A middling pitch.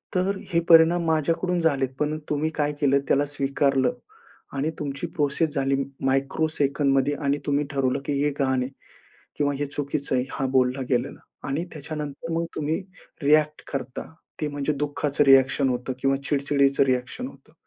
Yes: medium, 145 Hz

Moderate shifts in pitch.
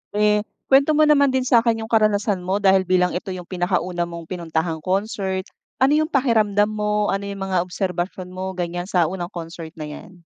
Yes: average, 3.1 semitones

